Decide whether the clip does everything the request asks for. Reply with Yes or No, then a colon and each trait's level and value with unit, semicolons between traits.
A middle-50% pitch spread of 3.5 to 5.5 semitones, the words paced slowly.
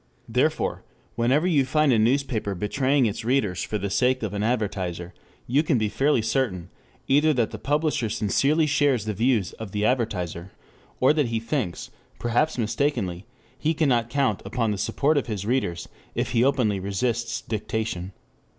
No: average, 4.8 semitones; average, 165 wpm